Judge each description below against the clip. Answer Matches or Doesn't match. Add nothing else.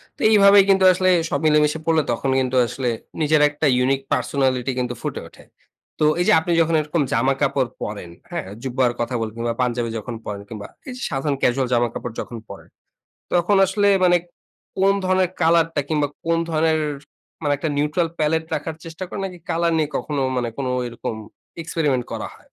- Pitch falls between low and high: Matches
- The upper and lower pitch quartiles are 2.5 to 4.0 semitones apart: Doesn't match